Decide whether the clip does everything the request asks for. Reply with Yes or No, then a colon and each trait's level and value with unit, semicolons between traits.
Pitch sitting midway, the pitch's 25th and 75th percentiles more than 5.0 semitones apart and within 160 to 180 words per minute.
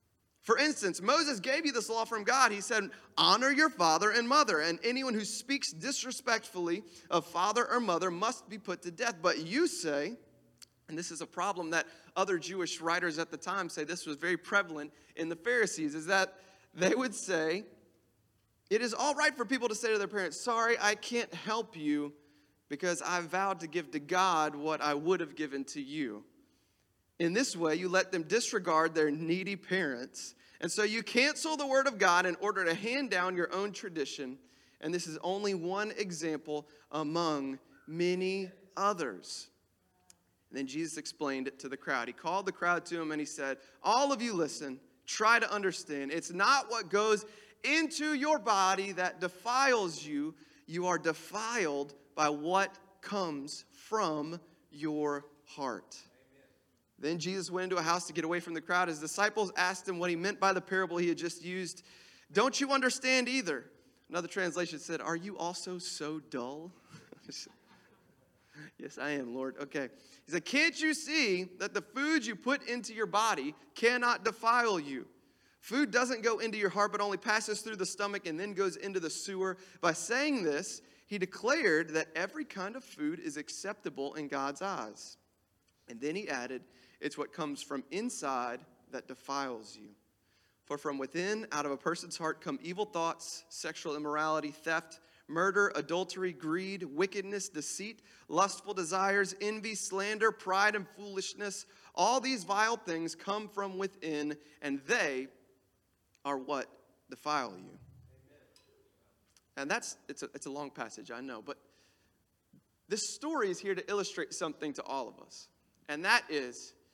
Yes: medium, 180 Hz; wide, 5.6 semitones; average, 170 wpm